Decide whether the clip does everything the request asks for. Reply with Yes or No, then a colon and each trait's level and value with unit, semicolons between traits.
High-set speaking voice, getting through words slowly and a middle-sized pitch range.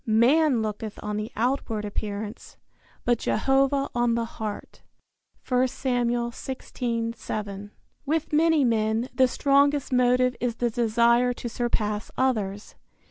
Yes: high, 240 Hz; slow, 120 wpm; average, 3.0 semitones